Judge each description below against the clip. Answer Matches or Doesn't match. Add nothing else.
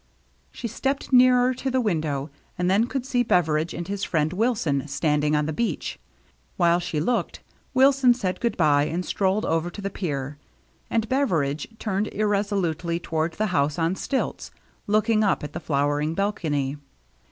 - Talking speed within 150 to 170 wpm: Matches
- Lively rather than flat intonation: Matches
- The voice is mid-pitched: Matches